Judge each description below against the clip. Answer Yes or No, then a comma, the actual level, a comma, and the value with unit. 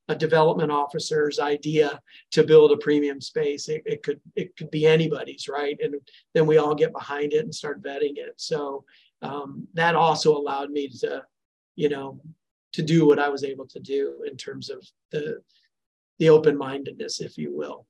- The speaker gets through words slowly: No, average, 180 wpm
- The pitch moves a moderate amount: No, wide, 6.8 semitones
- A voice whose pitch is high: No, medium, 155 Hz